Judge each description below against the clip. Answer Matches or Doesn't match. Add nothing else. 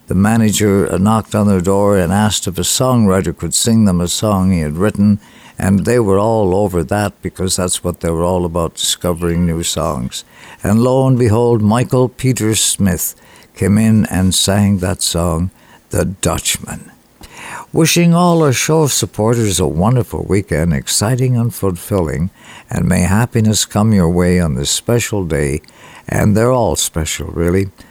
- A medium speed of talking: Matches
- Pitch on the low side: Matches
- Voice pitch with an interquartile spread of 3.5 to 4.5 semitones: Matches